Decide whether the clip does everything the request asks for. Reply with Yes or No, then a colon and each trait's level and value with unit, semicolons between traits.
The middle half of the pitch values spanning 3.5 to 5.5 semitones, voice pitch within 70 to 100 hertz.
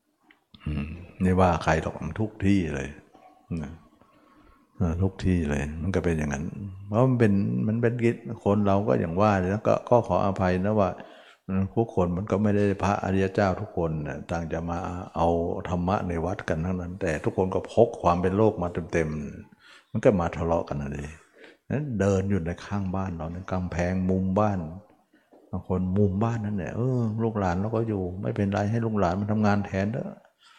No: average, 3.0 semitones; very low, 95 Hz